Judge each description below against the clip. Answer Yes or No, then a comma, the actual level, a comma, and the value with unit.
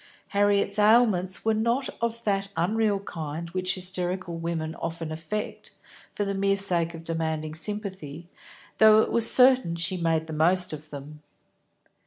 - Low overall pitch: No, medium, 185 Hz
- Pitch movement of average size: Yes, average, 4.0 semitones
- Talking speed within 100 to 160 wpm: Yes, average, 150 wpm